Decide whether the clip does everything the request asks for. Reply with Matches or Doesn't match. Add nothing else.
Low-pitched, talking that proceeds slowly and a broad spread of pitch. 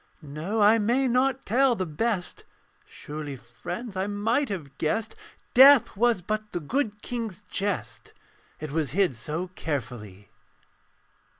Doesn't match